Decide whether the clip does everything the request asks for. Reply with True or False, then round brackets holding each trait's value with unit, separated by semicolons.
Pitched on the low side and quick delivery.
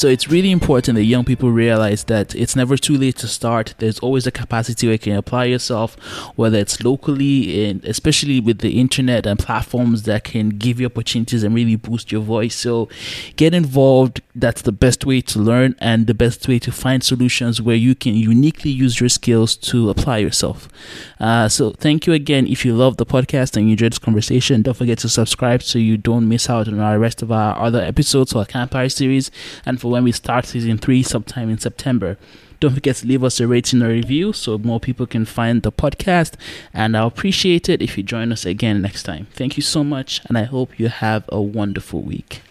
True (120 Hz; 215 wpm)